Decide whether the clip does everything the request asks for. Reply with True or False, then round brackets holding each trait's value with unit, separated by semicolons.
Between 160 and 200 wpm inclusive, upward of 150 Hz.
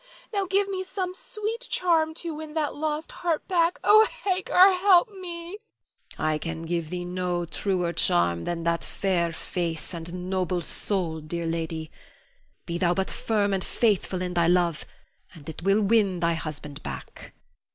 True (165 wpm; 185 Hz)